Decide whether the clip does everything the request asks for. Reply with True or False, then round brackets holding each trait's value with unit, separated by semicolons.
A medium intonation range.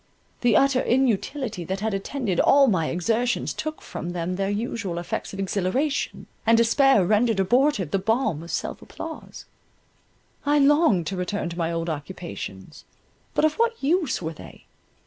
False (7.2 semitones)